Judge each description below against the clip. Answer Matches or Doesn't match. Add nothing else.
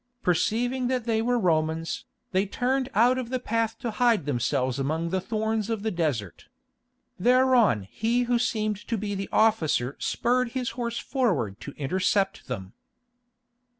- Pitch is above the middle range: Matches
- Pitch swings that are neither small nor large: Doesn't match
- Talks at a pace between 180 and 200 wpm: Doesn't match